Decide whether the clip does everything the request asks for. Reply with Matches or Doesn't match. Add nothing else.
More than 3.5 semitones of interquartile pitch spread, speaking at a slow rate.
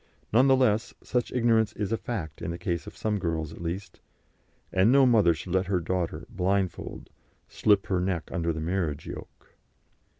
Doesn't match